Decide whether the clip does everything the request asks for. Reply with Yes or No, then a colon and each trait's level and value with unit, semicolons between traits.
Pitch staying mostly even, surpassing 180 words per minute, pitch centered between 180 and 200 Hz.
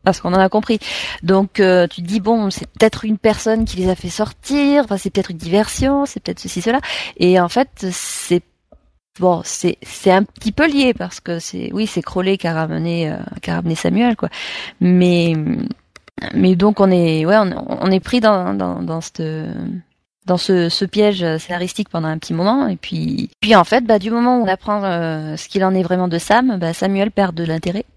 No: average, 3.7 semitones; fast, 220 wpm; high, 190 Hz